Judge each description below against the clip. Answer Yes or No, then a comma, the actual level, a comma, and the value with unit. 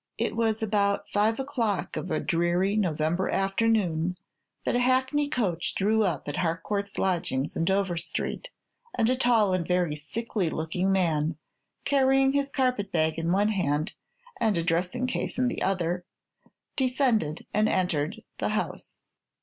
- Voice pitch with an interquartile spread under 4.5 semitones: No, average, 5.3 semitones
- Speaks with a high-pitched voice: Yes, high, 195 Hz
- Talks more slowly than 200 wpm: Yes, average, 150 wpm